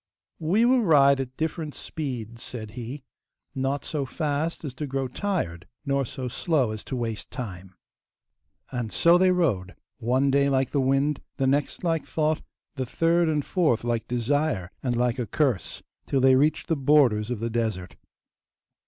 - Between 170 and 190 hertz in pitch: No, low, 135 Hz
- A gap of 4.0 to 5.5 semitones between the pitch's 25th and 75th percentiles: Yes, average, 4.3 semitones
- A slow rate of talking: No, average, 170 wpm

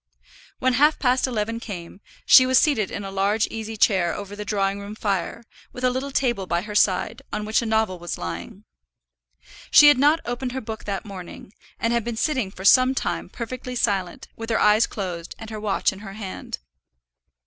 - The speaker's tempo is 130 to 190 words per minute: No, average, 200 wpm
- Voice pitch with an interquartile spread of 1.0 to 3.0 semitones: No, average, 4.1 semitones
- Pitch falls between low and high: No, high, 220 Hz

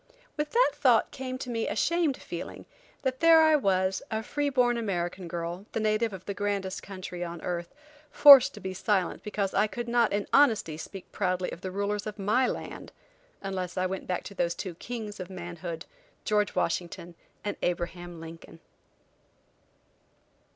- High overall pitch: Yes, high, 200 Hz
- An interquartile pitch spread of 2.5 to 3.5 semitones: No, average, 4.7 semitones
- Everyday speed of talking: Yes, average, 170 wpm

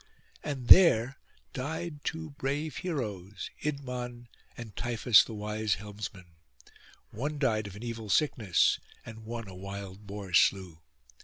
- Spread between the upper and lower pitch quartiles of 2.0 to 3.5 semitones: No, average, 5.1 semitones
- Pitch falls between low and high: No, low, 115 Hz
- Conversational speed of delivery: No, slow, 130 wpm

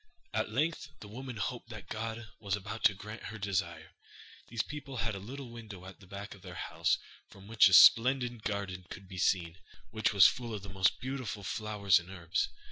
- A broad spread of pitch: No, average, 3.3 semitones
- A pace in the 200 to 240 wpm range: Yes, fast, 205 wpm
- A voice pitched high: No, low, 105 Hz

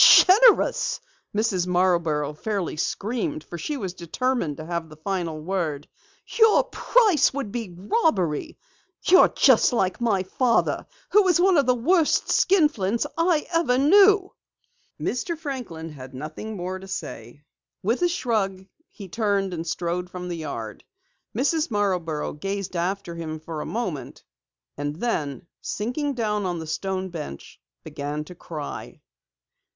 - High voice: Yes, high, 195 Hz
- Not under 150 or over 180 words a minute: No, average, 140 wpm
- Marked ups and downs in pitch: Yes, wide, 7.6 semitones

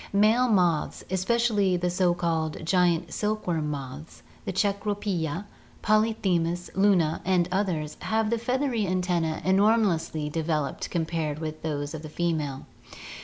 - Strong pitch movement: No, average, 4.3 semitones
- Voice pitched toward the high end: No, medium, 175 Hz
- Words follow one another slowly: Yes, slow, 130 wpm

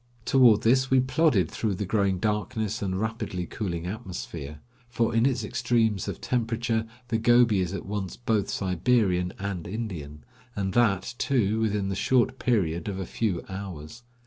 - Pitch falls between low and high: No, low, 105 Hz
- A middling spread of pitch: Yes, average, 3.9 semitones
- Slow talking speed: No, average, 160 wpm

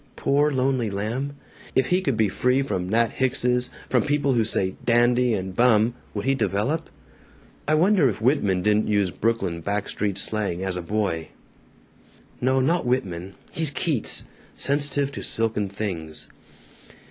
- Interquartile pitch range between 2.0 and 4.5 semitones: No, average, 5.3 semitones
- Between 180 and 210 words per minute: No, average, 150 wpm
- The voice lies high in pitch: No, low, 115 Hz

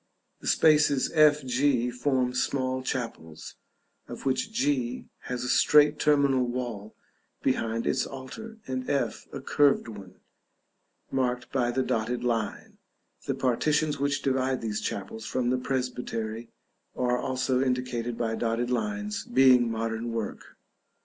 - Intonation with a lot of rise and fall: No, average, 3.0 semitones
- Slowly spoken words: Yes, slow, 130 wpm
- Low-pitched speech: Yes, low, 130 Hz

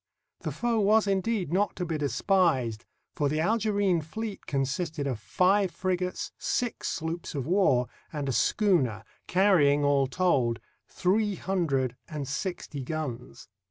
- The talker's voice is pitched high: No, medium, 170 Hz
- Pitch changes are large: Yes, wide, 5.8 semitones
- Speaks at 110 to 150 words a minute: Yes, slow, 135 wpm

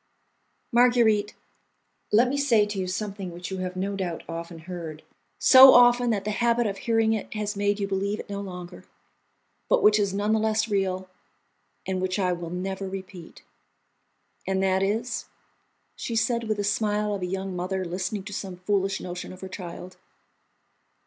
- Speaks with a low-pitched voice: No, high, 195 Hz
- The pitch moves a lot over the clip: No, narrow, 2.6 semitones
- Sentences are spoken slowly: No, average, 175 wpm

